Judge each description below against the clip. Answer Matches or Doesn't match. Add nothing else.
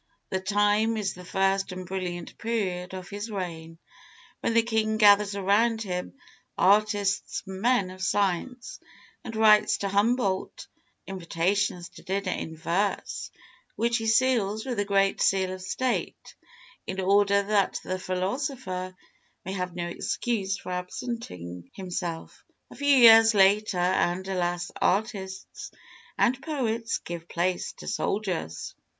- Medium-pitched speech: Doesn't match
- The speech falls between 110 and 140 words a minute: Matches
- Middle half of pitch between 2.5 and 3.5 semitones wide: Matches